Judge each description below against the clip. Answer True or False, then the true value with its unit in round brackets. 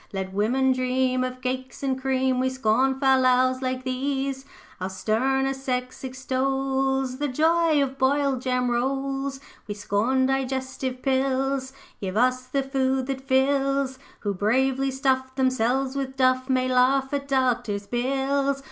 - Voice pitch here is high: True (260 Hz)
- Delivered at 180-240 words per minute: False (140 wpm)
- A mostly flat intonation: True (1.0 semitones)